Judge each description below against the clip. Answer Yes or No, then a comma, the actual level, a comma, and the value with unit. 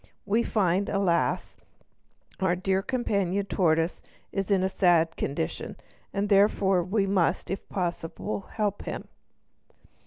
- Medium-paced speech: No, slow, 125 wpm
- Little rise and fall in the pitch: Yes, narrow, 2.3 semitones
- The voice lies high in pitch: Yes, high, 195 Hz